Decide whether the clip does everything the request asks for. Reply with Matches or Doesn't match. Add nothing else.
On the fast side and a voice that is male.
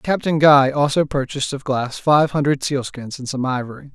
Doesn't match